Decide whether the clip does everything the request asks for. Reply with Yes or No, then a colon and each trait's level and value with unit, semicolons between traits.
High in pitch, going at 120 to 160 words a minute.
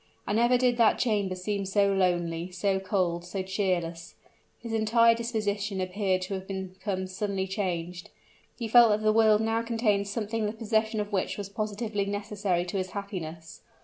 No: high, 200 Hz; average, 170 wpm